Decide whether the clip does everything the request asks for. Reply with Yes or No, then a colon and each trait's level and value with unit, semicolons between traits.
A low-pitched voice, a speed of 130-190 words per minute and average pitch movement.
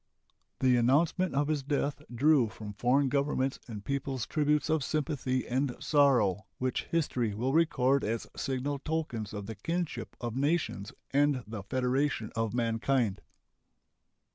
Yes: low, 130 Hz; average, 140 wpm; average, 3.9 semitones